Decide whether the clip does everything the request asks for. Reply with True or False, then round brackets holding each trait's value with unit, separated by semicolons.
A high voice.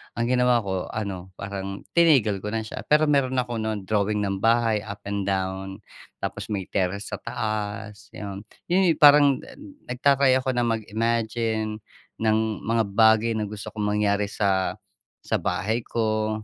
False (110 Hz)